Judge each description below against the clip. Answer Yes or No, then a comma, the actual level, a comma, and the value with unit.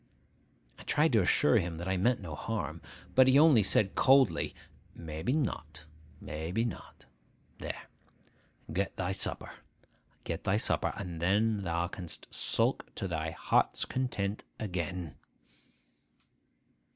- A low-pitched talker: Yes, very low, 95 Hz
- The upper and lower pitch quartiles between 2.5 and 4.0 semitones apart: No, average, 5.0 semitones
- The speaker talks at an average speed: No, slow, 125 wpm